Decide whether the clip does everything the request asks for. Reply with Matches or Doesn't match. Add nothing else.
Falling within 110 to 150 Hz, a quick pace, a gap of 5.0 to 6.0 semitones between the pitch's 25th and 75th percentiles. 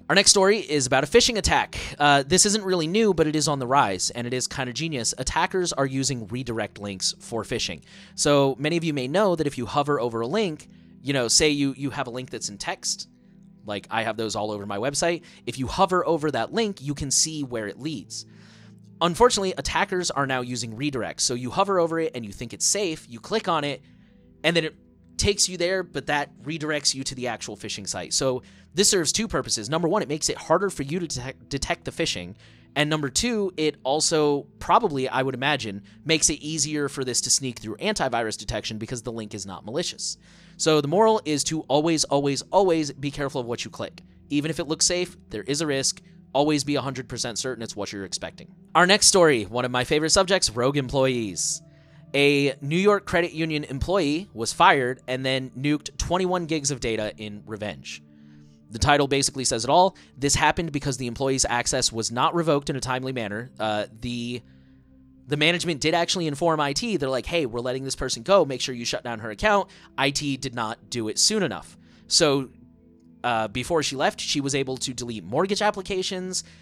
Matches